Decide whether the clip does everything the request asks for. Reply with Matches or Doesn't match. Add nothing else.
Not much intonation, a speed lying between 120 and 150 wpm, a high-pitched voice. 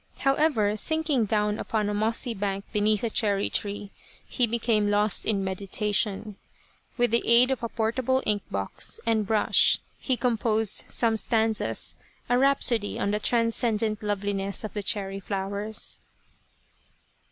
Matches